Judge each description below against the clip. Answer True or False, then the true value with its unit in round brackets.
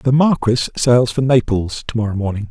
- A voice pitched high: False (120 Hz)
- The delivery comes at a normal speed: True (190 wpm)